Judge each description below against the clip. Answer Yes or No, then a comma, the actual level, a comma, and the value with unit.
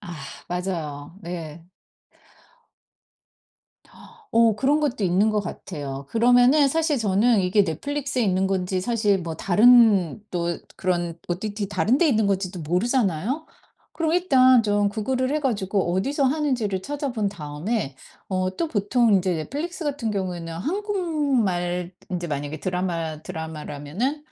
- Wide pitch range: Yes, wide, 6.5 semitones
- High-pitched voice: Yes, high, 200 Hz